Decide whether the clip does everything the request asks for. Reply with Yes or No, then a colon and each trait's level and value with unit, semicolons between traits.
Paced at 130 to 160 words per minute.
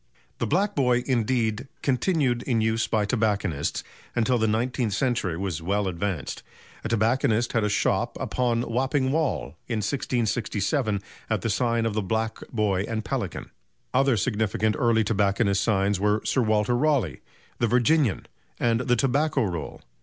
Yes: average, 150 wpm